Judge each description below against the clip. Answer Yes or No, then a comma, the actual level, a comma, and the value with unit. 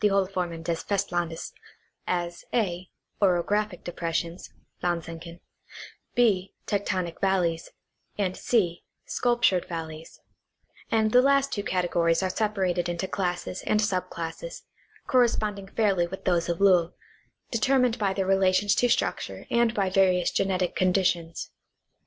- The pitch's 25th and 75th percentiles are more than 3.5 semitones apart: No, average, 3.1 semitones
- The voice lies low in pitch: No, medium, 185 Hz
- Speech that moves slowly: Yes, slow, 120 wpm